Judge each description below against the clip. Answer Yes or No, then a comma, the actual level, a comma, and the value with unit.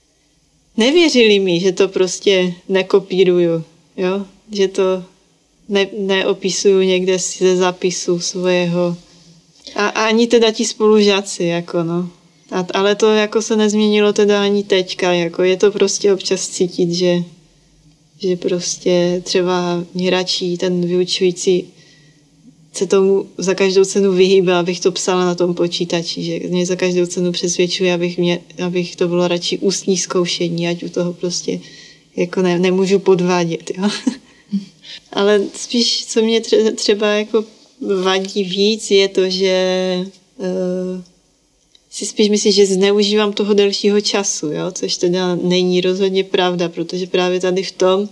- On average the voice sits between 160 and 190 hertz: Yes, medium, 185 Hz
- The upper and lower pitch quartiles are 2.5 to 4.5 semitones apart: No, narrow, 2.1 semitones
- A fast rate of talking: No, average, 140 wpm